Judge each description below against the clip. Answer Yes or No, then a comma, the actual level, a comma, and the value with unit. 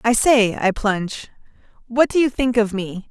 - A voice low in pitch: No, high, 225 Hz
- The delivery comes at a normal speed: Yes, average, 195 wpm